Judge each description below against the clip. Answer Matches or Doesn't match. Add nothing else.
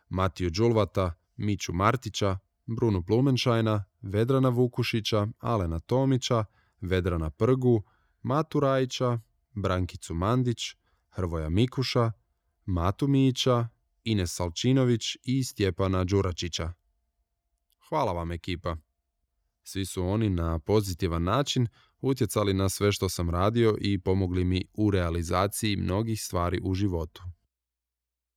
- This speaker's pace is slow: Matches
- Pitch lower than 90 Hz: Doesn't match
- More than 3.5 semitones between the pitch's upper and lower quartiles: Matches